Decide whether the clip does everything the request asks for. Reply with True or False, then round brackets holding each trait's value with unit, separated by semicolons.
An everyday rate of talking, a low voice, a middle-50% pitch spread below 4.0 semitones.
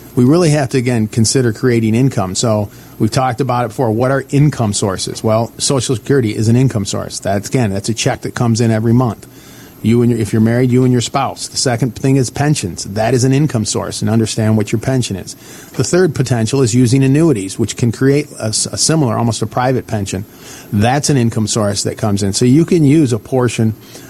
False (225 wpm; 120 Hz; 3.5 semitones)